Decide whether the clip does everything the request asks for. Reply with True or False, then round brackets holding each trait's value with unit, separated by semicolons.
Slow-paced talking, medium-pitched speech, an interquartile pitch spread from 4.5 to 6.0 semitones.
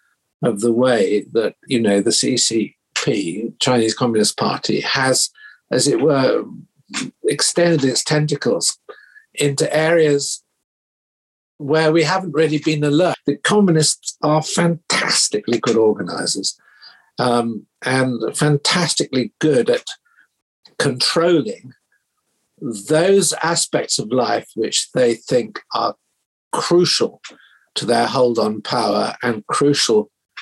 True (105 wpm; 145 Hz; 5.5 semitones)